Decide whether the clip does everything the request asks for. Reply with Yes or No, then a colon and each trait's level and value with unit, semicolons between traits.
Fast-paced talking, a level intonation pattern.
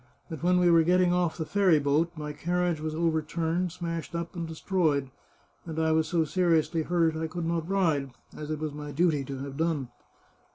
Yes: fast, 210 wpm; narrow, 2.1 semitones